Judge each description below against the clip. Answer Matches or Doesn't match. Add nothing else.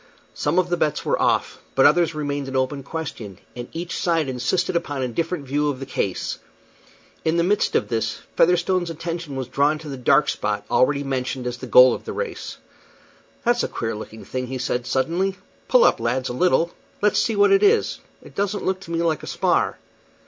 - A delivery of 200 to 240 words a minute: Matches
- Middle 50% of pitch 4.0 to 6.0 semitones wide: Matches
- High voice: Doesn't match